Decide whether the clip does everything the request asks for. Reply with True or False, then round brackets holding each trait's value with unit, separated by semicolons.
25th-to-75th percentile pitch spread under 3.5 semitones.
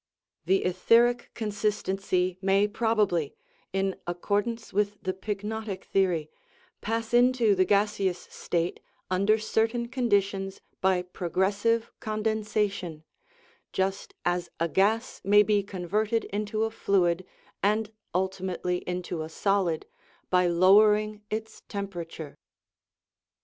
True (2.8 semitones)